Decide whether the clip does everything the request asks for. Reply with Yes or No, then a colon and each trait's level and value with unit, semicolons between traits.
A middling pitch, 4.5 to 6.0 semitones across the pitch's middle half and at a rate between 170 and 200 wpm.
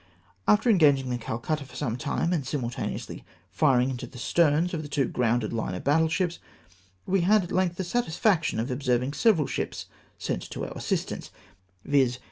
Yes: medium, 145 Hz; wide, 5.6 semitones; average, 180 wpm